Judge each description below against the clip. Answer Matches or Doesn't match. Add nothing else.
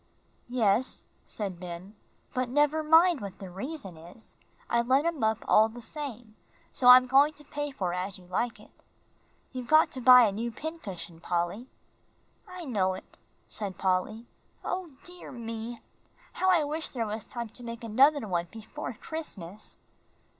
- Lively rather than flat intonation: Matches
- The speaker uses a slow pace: Doesn't match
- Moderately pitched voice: Doesn't match